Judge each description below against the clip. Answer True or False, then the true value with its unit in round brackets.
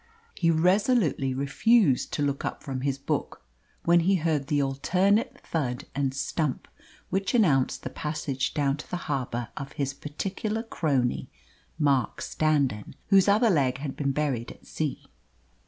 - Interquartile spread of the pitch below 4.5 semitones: False (4.8 semitones)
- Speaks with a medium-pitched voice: True (145 Hz)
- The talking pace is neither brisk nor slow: True (150 wpm)